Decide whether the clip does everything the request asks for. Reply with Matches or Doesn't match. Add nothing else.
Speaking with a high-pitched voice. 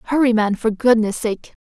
Matches